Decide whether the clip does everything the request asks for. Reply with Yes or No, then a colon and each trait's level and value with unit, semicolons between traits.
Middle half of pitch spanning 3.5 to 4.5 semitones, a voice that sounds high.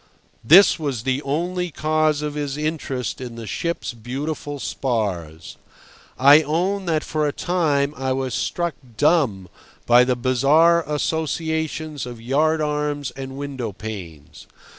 No: average, 4.0 semitones; medium, 145 Hz